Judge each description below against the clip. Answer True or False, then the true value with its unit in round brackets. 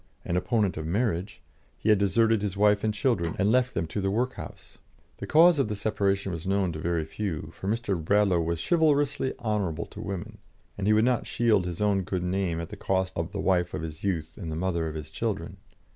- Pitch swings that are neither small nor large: True (4.1 semitones)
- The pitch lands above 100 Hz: False (95 Hz)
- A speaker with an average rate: False (230 wpm)